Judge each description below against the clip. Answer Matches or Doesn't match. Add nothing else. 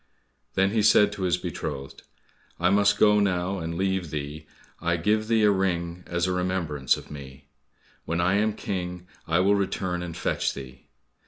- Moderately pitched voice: Doesn't match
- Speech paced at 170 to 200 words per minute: Matches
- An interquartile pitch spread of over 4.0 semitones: Doesn't match